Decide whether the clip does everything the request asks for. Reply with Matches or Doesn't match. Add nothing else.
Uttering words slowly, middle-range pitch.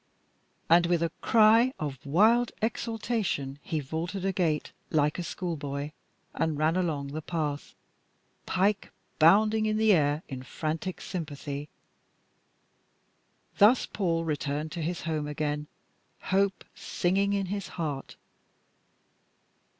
Matches